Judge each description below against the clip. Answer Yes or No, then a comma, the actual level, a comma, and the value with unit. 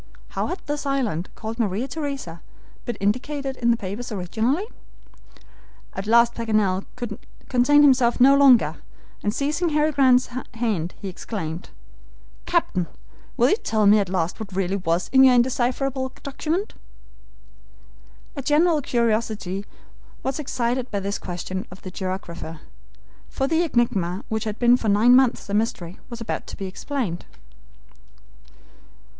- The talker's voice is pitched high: Yes, high, 235 Hz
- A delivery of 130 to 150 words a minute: Yes, average, 140 wpm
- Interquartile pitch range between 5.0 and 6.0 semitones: Yes, average, 5.3 semitones